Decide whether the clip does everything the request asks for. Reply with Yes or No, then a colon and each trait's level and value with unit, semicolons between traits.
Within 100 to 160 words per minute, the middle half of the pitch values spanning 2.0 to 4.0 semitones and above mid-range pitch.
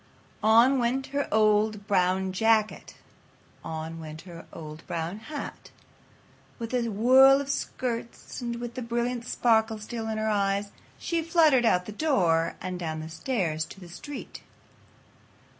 No: average, 145 wpm; average, 5.1 semitones; high, 220 Hz